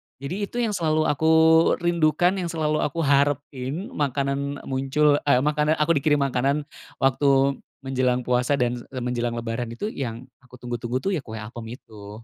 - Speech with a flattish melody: No, average, 3.5 semitones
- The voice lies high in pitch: No, medium, 140 Hz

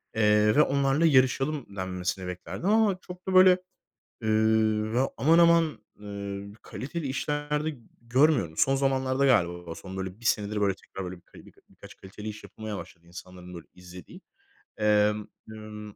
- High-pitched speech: No, low, 110 Hz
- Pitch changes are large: Yes, wide, 5.9 semitones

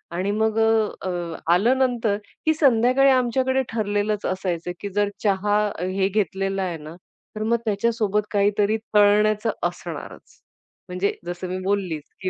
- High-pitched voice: Yes, high, 205 Hz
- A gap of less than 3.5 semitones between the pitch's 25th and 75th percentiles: Yes, average, 2.8 semitones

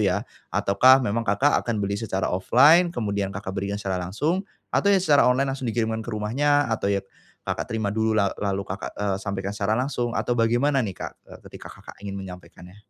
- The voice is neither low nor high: No, low, 110 Hz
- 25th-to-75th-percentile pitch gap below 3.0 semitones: No, average, 4.2 semitones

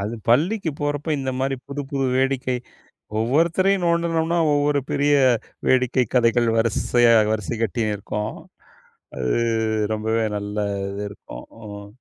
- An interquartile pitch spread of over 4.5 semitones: Yes, average, 5.1 semitones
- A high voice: No, low, 125 Hz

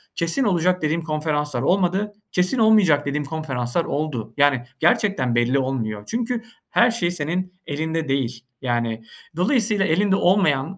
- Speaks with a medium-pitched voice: Yes, medium, 160 Hz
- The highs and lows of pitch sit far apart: Yes, wide, 5.9 semitones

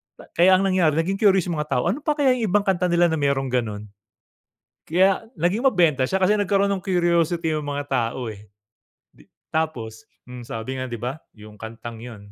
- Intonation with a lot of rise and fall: Yes, wide, 7.2 semitones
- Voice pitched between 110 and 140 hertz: No, medium, 160 Hz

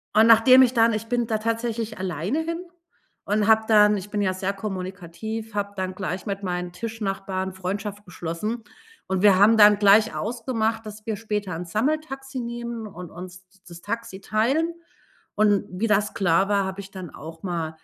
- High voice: Yes, high, 210 Hz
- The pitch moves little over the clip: No, average, 3.1 semitones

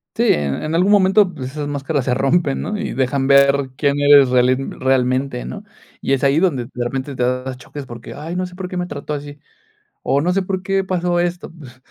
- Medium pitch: Yes, medium, 145 Hz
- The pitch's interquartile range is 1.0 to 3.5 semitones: No, average, 5.2 semitones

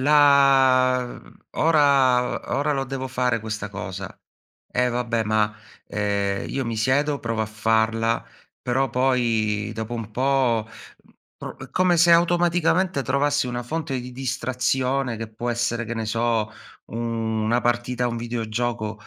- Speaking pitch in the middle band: No, low, 120 Hz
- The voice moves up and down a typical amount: Yes, average, 3.2 semitones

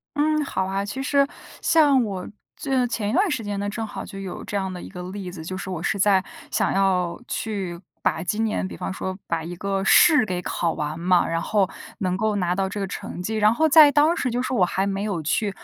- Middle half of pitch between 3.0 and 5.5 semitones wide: Yes, average, 4.2 semitones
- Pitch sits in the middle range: No, high, 195 Hz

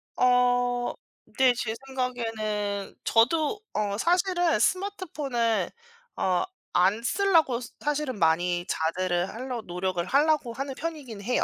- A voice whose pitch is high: Yes, high, 245 Hz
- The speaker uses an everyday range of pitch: No, wide, 6.2 semitones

